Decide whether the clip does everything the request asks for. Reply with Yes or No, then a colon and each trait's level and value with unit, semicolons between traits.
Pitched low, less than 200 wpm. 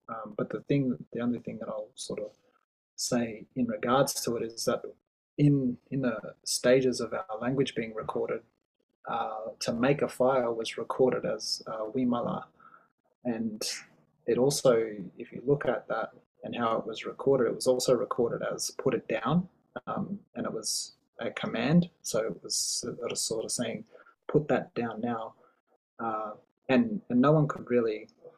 No: medium, 145 Hz; average, 180 wpm